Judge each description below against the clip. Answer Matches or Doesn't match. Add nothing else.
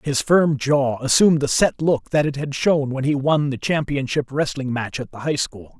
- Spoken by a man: Matches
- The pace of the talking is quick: Matches